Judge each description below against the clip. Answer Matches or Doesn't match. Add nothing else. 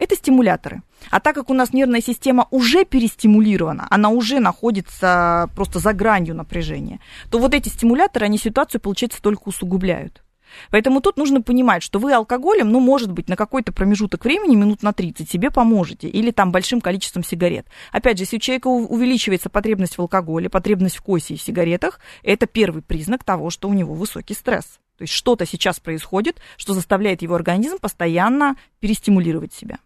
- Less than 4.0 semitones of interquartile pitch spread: Doesn't match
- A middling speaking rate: Doesn't match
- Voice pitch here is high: Matches